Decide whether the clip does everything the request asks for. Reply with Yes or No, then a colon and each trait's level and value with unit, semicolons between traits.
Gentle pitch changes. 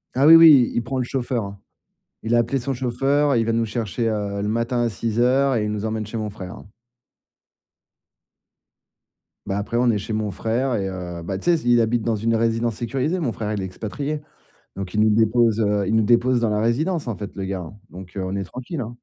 No: average, 3.0 semitones